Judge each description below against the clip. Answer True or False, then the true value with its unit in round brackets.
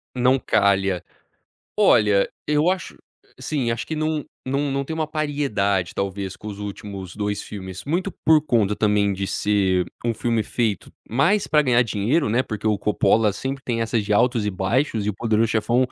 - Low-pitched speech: True (110 Hz)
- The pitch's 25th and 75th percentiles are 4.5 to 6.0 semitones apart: True (5.2 semitones)